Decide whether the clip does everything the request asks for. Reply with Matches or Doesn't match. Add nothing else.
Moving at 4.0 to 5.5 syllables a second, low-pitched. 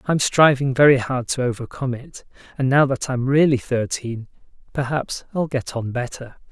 Matches